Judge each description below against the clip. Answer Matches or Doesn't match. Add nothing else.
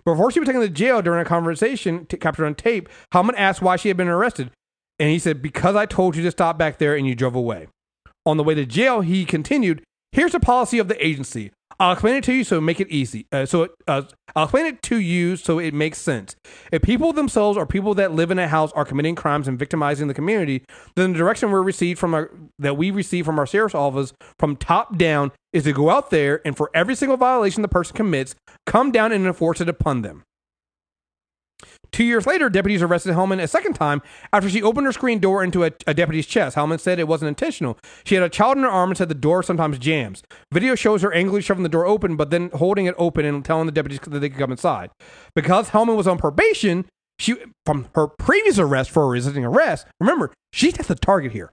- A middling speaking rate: Doesn't match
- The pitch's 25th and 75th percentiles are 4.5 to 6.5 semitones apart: Matches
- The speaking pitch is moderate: Matches